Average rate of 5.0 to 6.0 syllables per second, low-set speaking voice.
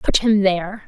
No: 5.3 syllables/s; high, 195 Hz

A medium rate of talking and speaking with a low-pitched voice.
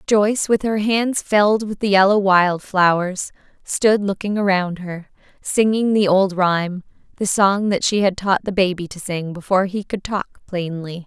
No: average, 180 wpm; high, 195 Hz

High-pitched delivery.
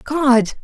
Yes: very high, 265 Hz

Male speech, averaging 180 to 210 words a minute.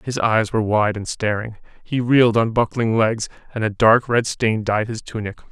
Yes: male; fast, 205 wpm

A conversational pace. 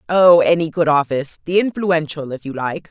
Yes: average, 165 wpm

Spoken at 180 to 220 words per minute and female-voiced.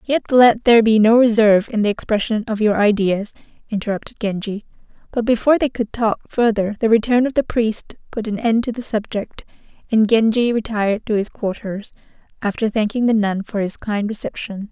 Yes: average, 185 wpm; female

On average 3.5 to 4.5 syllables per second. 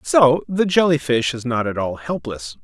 Yes: 4.4 syllables/s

